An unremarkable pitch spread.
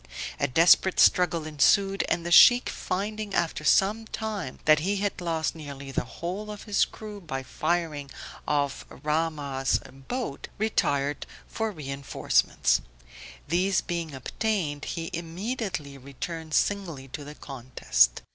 No: wide, 5.7 semitones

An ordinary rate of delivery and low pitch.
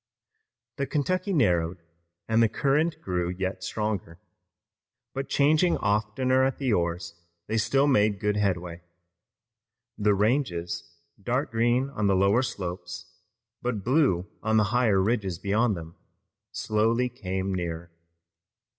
No: slow, 125 wpm; low, 105 Hz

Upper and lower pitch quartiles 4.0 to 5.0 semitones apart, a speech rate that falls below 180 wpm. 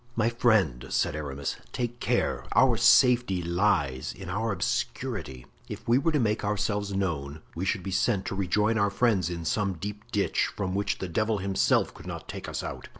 No: average, 4.3 semitones; average, 190 wpm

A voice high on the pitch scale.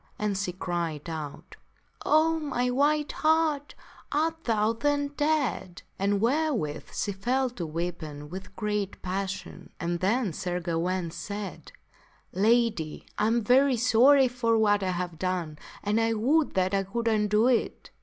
Yes: high, 210 Hz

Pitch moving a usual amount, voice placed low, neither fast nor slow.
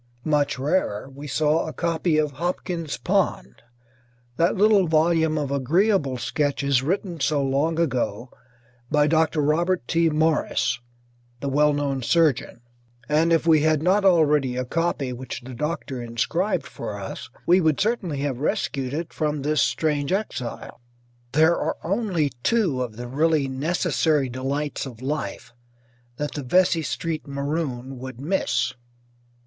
No: average, 3.7 semitones; medium, 150 Hz; average, 145 wpm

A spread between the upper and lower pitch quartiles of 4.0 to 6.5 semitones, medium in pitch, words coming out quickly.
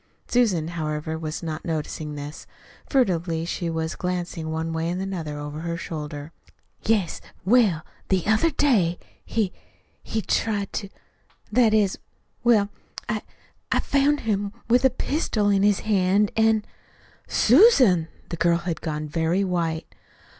No: average, 5.1 semitones; medium, 180 Hz; average, 140 wpm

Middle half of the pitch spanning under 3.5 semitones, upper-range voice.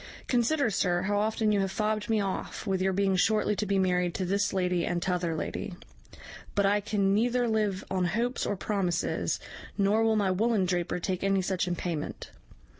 Yes: narrow, 2.6 semitones; high, 195 Hz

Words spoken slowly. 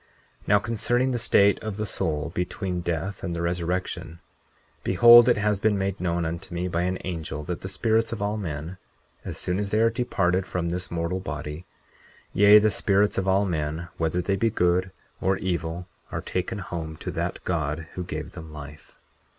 No: average, 190 wpm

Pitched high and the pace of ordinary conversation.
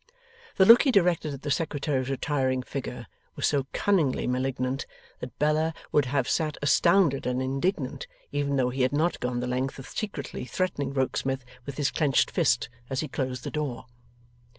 No: medium, 140 Hz; average, 175 wpm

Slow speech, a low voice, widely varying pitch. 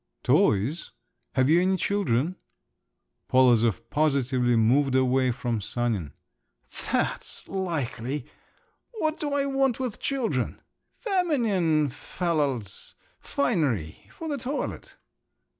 No: slow, 95 wpm; medium, 145 Hz; wide, 8.9 semitones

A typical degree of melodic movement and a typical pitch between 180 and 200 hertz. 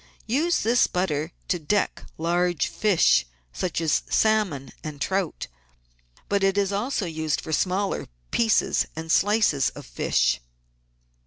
Yes: average, 4.6 semitones; medium, 185 Hz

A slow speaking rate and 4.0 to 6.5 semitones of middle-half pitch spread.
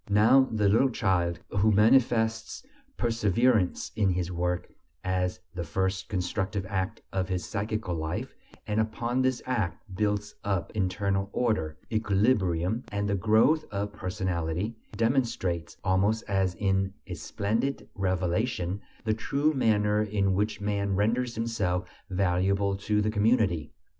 No: slow, 130 wpm; average, 3.1 semitones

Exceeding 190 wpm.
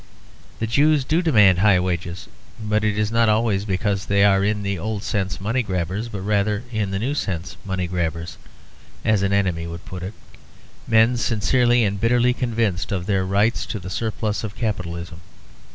No: average, 180 wpm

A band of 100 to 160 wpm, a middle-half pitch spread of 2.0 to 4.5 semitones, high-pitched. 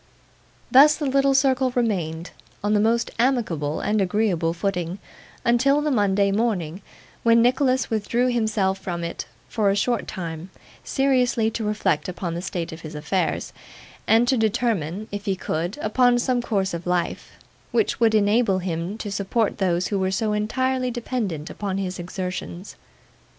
No: average, 155 wpm; average, 4.9 semitones; high, 210 Hz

